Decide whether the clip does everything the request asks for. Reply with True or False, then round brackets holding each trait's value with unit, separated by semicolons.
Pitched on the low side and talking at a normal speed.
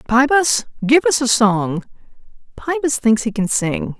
False (245 Hz; 150 wpm)